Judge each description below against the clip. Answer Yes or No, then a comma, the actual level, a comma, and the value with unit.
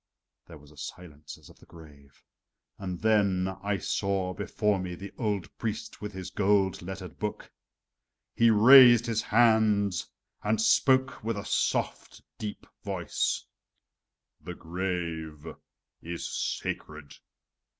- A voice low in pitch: Yes, very low, 95 Hz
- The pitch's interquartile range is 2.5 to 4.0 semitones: Yes, average, 3.7 semitones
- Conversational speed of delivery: No, slow, 125 wpm